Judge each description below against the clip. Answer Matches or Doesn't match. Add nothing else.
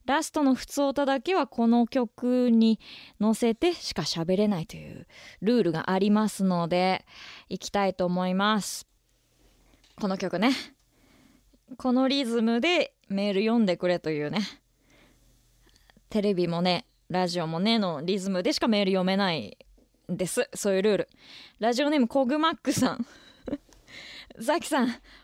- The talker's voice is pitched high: Matches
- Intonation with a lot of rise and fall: Matches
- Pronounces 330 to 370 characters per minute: Doesn't match